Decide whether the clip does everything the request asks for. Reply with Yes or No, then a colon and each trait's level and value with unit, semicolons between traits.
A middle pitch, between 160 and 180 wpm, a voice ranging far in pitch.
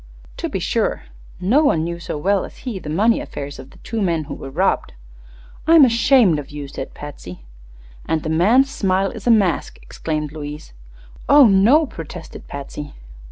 Yes: medium, 175 Hz; average, 175 wpm; wide, 7.4 semitones